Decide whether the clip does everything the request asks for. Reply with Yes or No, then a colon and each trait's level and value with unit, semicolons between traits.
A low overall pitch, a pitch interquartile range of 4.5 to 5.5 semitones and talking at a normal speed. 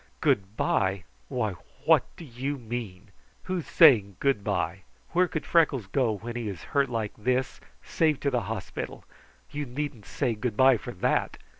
Yes: low, 120 Hz; average, 5.2 semitones; average, 165 wpm